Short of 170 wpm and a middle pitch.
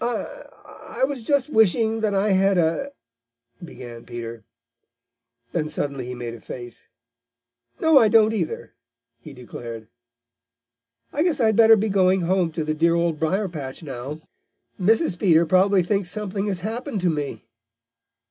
Yes: average, 155 wpm; medium, 180 Hz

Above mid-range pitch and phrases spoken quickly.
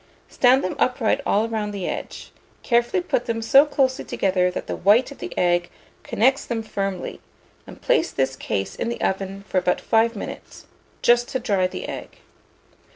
No: high, 225 Hz; average, 175 wpm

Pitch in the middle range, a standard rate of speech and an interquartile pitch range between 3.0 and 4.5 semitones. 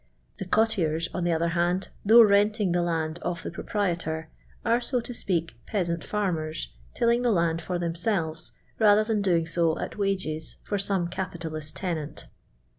Yes: medium, 175 Hz; average, 165 wpm; average, 3.8 semitones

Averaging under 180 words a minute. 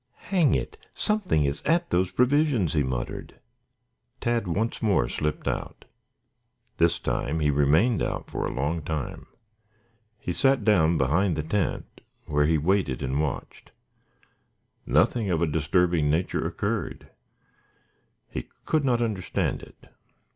Yes: slow, 135 wpm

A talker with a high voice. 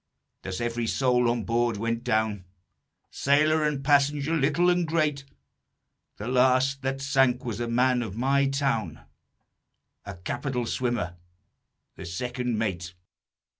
No: low, 125 Hz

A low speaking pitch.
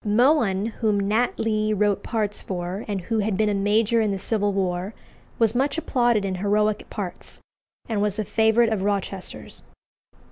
No: high, 210 Hz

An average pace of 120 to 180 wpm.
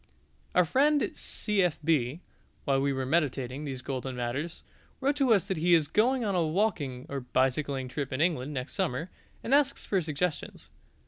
Yes: average, 170 wpm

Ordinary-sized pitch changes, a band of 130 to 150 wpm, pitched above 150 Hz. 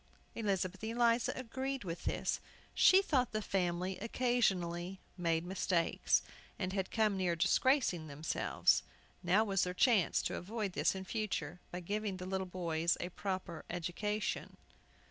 Yes: average, 3.8 semitones; average, 140 wpm; high, 190 Hz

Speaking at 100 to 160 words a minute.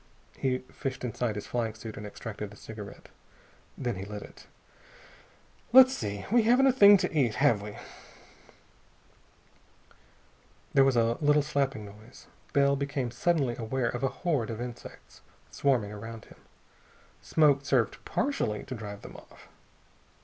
Yes: average, 145 wpm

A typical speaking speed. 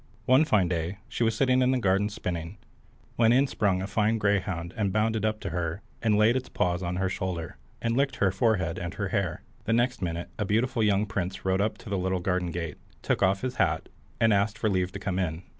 No: fast, 230 wpm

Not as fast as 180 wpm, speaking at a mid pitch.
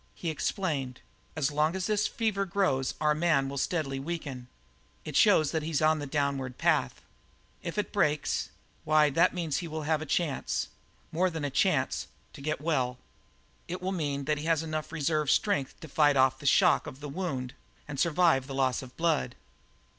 No: average, 190 wpm; medium, 155 Hz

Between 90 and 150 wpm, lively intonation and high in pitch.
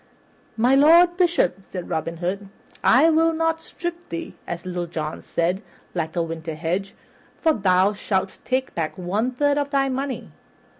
No: average, 160 wpm; wide, 8.7 semitones; high, 200 Hz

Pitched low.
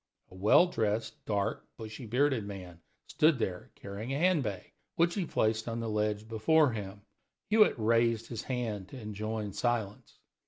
Yes: low, 110 Hz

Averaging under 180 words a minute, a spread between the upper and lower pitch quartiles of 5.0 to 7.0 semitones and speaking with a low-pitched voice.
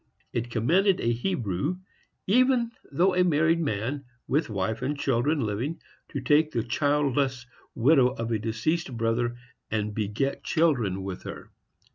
Yes: average, 140 wpm; wide, 5.6 semitones; low, 130 Hz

